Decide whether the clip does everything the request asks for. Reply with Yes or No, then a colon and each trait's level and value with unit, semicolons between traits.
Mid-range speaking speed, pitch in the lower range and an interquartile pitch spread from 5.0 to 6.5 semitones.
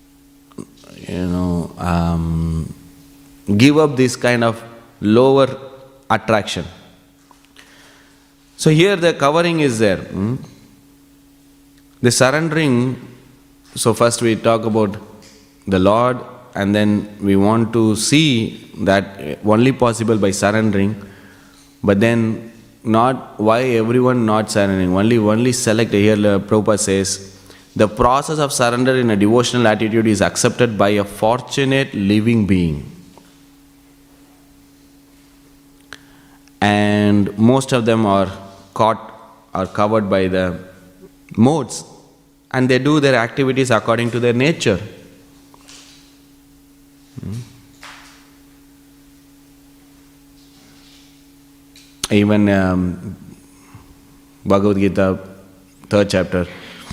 No: slow, 95 wpm; low, 120 Hz; wide, 5.6 semitones